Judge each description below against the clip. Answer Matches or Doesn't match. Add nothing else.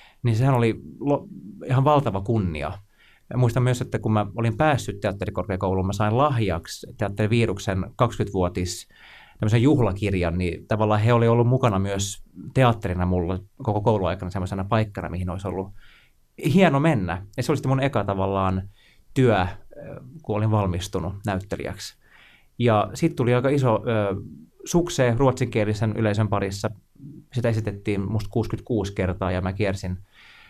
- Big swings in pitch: Doesn't match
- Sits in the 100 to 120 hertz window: Matches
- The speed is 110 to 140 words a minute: Matches